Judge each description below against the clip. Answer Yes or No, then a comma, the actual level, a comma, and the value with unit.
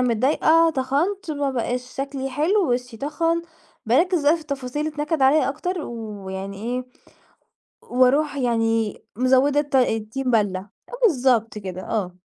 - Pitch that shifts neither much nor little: Yes, average, 4.7 semitones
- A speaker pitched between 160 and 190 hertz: No, very high, 260 Hz